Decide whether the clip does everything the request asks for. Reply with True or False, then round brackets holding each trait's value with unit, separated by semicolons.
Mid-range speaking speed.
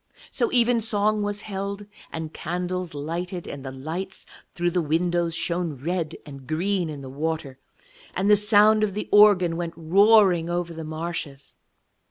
True (155 wpm)